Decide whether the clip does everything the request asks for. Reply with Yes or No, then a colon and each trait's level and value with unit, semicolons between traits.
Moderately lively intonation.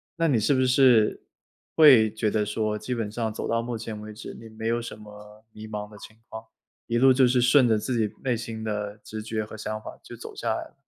No: narrow, 2.1 semitones